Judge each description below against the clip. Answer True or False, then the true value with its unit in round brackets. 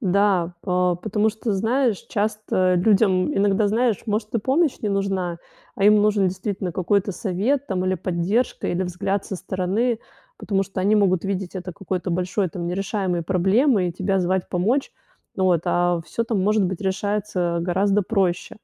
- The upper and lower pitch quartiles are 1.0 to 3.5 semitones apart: True (2.5 semitones)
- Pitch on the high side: True (195 Hz)